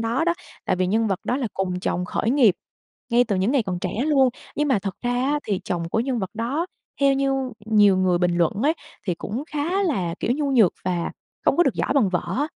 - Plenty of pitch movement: Yes, wide, 6.7 semitones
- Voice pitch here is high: Yes, high, 225 Hz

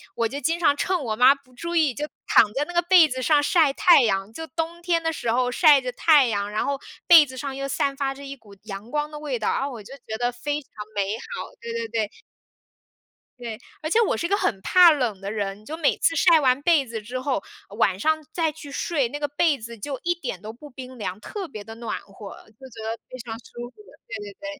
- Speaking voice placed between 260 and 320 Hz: Yes, very high, 270 Hz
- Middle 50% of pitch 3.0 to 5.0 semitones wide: No, wide, 5.4 semitones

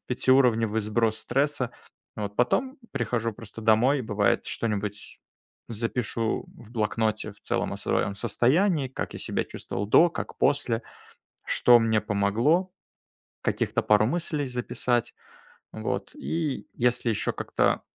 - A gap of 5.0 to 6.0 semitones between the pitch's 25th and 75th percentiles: No, average, 3.3 semitones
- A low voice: Yes, low, 115 Hz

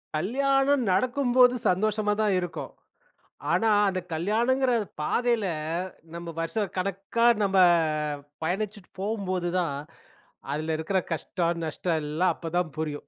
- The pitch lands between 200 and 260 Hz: No, high, 190 Hz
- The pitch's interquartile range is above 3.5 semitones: Yes, average, 4.8 semitones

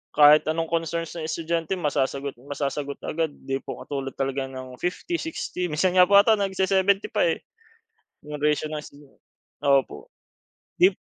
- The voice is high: No, medium, 155 Hz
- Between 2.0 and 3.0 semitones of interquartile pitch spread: No, average, 4.4 semitones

